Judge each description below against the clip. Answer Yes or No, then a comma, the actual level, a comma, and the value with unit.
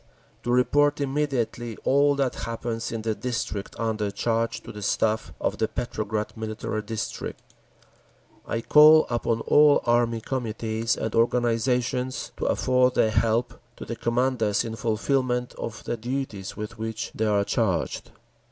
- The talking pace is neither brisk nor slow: Yes, average, 145 wpm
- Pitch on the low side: Yes, low, 115 Hz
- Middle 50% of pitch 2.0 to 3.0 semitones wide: Yes, narrow, 2.4 semitones